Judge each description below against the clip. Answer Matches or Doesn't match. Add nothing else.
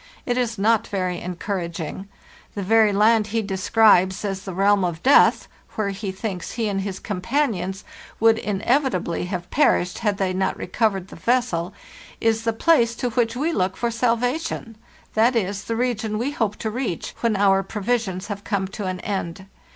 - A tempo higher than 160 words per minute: Matches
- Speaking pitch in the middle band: Doesn't match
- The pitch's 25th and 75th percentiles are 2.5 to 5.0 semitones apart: Matches